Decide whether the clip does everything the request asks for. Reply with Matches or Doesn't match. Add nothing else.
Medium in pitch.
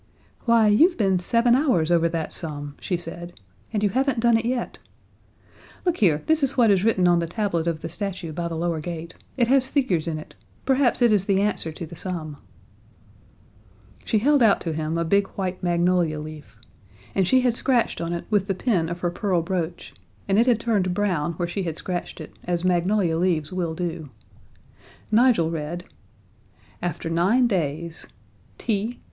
Matches